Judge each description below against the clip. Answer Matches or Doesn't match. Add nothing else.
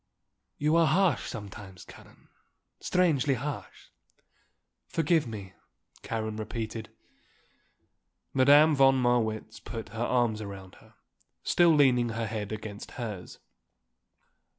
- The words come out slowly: Matches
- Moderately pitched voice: Doesn't match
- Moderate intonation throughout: Matches